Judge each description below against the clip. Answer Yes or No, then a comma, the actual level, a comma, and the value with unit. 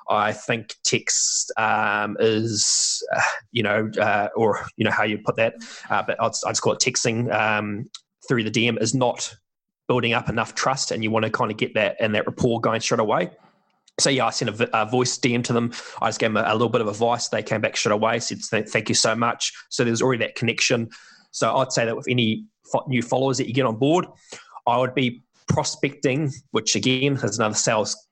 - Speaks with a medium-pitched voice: No, low, 120 Hz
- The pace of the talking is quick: Yes, fast, 225 wpm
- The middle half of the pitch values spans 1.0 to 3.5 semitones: Yes, average, 2.8 semitones